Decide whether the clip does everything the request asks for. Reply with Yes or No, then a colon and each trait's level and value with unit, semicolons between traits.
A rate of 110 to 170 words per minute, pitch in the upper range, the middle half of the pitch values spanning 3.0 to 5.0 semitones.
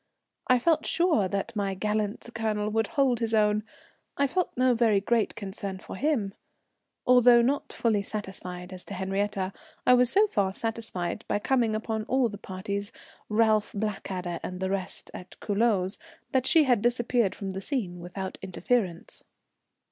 Yes: average, 160 wpm; high, 215 Hz; average, 3.7 semitones